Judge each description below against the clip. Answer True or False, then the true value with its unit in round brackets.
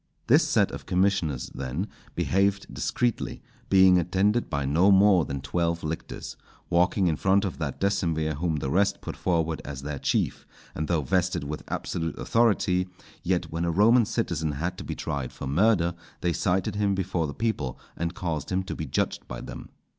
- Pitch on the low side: True (85 Hz)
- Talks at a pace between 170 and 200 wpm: True (180 wpm)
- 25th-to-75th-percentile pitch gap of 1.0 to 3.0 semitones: False (3.8 semitones)